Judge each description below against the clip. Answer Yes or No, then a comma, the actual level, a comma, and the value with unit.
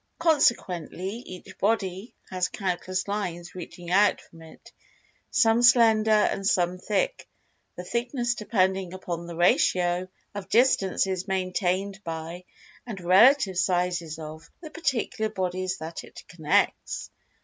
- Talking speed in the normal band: No, slow, 115 wpm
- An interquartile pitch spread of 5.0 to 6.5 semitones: No, average, 3.5 semitones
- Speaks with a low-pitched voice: No, medium, 185 Hz